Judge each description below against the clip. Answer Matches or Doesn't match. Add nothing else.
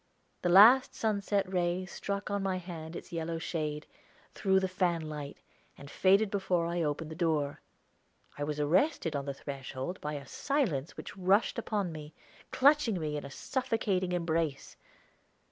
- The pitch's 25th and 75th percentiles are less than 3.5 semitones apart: Doesn't match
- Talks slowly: Doesn't match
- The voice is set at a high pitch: Doesn't match